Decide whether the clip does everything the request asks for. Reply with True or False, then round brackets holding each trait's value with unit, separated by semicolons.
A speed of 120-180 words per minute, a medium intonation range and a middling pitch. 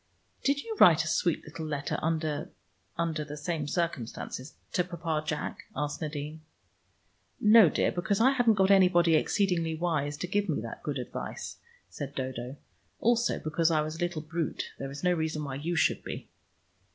True (175 wpm; 3.2 semitones; 160 Hz)